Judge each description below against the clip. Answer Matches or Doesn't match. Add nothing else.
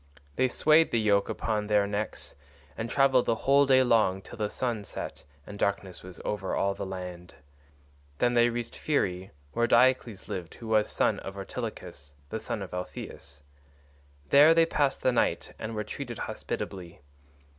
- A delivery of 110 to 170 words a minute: Matches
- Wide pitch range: Doesn't match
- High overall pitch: Doesn't match